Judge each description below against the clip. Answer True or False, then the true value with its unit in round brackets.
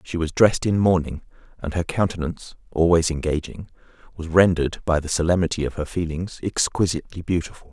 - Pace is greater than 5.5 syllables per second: True (6.1 syllables/s)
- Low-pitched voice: True (85 Hz)